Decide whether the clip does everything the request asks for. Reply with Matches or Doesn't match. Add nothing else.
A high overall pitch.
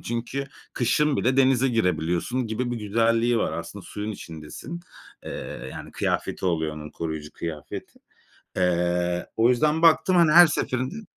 Doesn't match